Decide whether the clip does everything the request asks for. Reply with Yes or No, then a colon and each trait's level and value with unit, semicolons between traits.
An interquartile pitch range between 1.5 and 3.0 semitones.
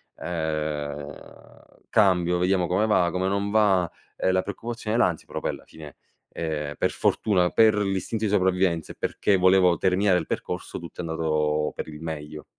No: average, 3.6 semitones